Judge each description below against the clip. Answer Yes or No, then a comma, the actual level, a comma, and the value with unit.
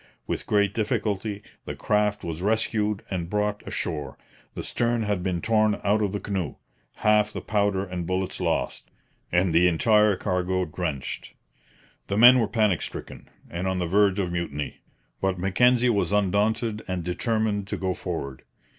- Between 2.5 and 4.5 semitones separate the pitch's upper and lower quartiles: Yes, average, 2.9 semitones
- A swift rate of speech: No, average, 160 wpm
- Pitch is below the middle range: Yes, low, 100 Hz